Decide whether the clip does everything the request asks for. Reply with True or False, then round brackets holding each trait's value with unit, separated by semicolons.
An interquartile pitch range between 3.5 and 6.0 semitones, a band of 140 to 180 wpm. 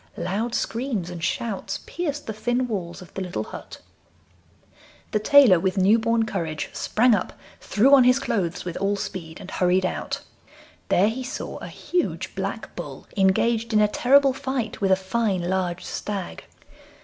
True (4.6 semitones; 165 wpm)